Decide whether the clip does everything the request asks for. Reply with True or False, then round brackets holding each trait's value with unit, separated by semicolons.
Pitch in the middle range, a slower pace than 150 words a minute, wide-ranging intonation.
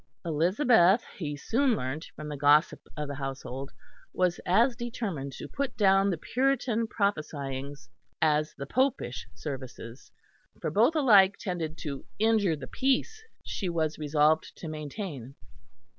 True (160 Hz; 135 wpm; 7.2 semitones)